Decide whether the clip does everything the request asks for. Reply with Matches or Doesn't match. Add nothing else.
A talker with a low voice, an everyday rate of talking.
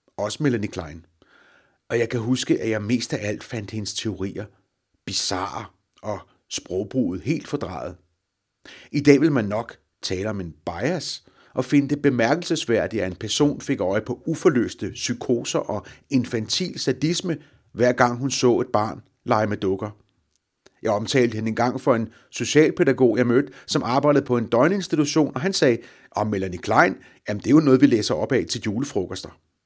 Matches